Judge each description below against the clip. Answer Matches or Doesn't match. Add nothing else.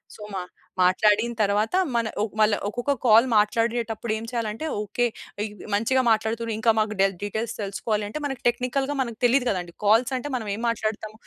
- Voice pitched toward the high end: Matches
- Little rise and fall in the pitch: Matches